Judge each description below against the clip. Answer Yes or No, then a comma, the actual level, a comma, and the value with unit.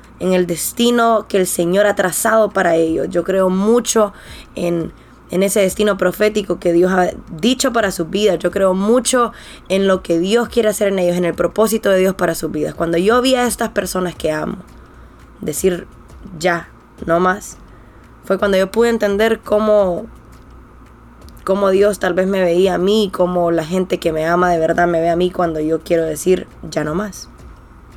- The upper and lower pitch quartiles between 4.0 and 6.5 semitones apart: No, average, 3.3 semitones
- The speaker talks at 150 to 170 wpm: No, fast, 190 wpm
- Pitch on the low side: No, medium, 185 Hz